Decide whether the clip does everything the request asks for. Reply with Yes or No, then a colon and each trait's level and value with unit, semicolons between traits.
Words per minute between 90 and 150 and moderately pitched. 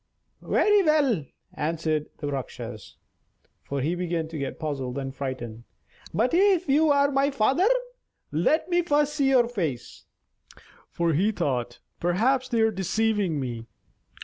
Yes: average, 140 wpm; medium, 180 Hz